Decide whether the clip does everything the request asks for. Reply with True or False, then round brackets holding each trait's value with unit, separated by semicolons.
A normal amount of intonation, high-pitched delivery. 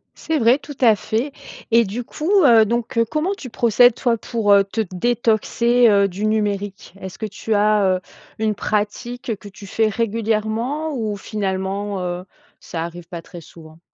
True (3.0 semitones; 215 Hz)